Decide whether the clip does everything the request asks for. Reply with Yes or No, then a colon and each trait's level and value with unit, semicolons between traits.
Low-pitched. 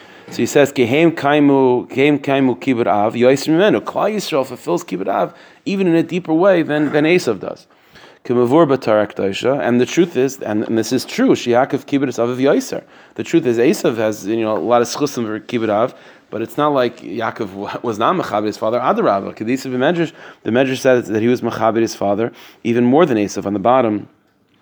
Yes: low, 125 Hz